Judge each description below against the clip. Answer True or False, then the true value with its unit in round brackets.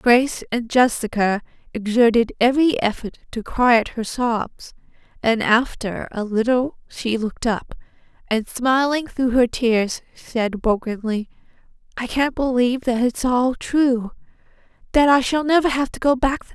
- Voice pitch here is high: True (245 Hz)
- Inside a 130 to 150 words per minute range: True (145 wpm)